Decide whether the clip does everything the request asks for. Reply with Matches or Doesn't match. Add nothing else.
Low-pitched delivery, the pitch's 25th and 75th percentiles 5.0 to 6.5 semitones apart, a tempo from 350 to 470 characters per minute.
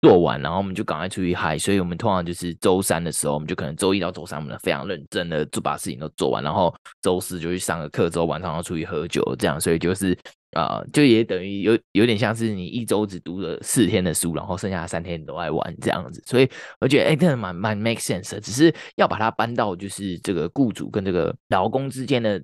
Doesn't match